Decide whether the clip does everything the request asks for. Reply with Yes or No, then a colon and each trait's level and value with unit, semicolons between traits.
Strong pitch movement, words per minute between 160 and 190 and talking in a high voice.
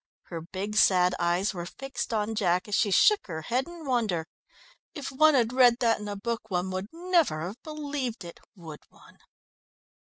Yes: wide, 6.5 semitones; average, 185 wpm; high, 215 Hz